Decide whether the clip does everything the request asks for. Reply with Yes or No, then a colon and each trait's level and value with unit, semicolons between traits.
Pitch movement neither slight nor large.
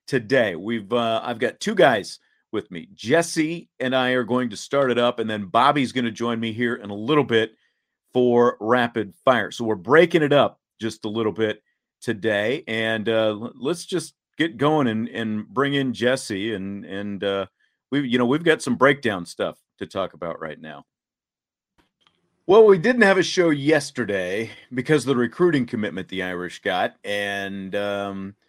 Yes: average, 4.6 semitones